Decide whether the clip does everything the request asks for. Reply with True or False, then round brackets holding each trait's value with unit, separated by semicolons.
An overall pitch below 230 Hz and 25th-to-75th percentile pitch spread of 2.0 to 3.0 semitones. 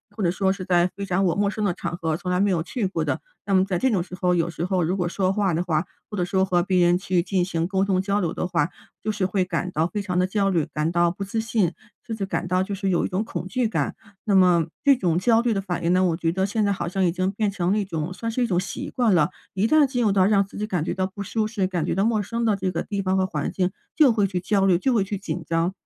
True (190 Hz; 2.5 semitones)